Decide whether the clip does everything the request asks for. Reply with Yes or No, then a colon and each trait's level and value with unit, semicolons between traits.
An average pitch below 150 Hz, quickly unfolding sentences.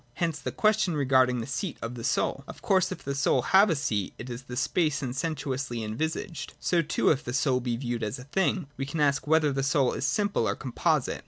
Yes: medium, 140 Hz; fast, 240 wpm